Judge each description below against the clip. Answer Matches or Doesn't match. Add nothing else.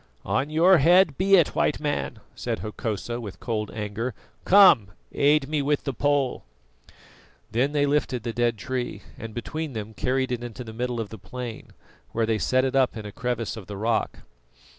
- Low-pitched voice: Matches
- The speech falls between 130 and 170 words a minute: Doesn't match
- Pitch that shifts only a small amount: Doesn't match